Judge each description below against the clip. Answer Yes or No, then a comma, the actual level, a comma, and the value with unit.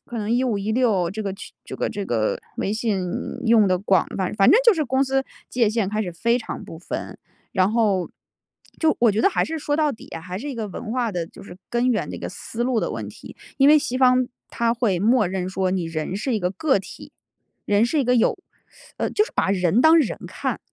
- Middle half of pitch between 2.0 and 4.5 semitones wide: No, average, 4.9 semitones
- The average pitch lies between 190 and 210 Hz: No, high, 220 Hz